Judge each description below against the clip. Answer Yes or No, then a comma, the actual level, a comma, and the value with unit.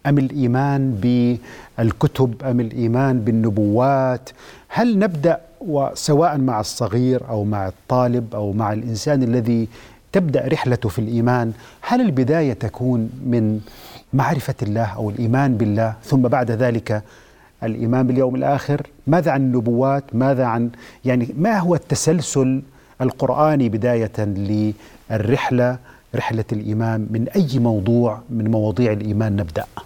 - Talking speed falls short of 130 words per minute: Yes, average, 115 wpm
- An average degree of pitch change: Yes, average, 3.2 semitones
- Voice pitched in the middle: No, low, 125 Hz